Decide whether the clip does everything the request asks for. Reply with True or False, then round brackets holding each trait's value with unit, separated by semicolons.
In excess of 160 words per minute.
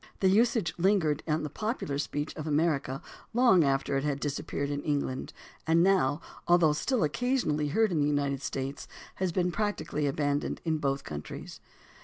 True (170 wpm)